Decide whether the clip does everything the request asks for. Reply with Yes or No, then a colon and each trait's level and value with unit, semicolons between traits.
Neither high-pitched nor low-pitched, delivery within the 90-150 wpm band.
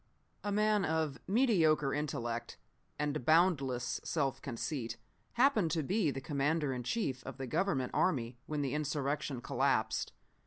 Yes: medium, 150 Hz; average, 140 wpm